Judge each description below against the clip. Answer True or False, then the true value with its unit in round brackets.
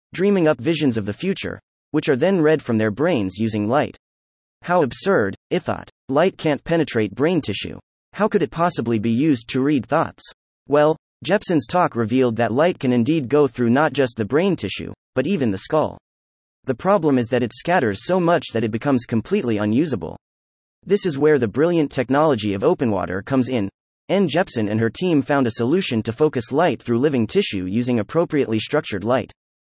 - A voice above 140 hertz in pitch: False (130 Hz)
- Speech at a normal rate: True (190 wpm)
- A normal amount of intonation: False (6.2 semitones)